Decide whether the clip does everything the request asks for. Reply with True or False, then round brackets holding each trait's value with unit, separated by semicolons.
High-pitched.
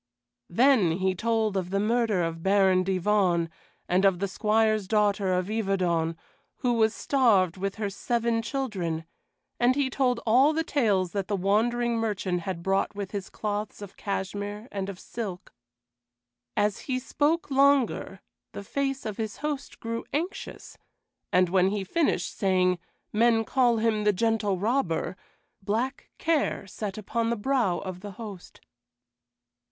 True (210 Hz)